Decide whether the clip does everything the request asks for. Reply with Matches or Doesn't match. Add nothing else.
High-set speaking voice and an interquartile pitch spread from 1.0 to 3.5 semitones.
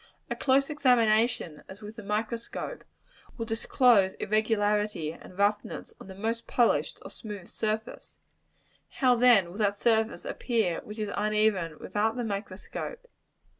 Matches